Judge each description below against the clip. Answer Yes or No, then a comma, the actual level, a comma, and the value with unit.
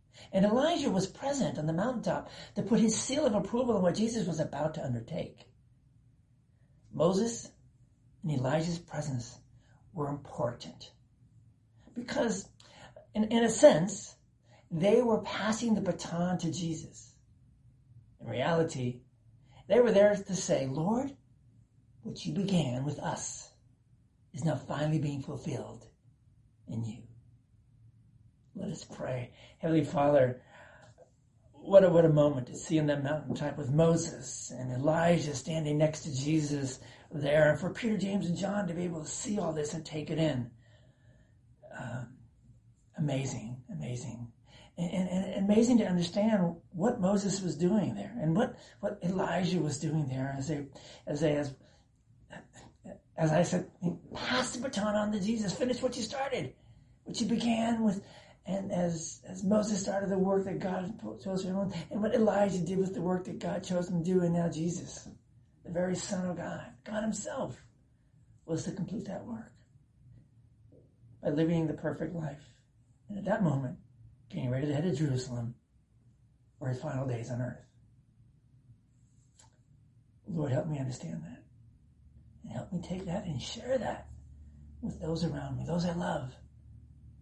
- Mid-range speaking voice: Yes, medium, 150 Hz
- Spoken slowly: No, average, 155 wpm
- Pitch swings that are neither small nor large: No, wide, 6.9 semitones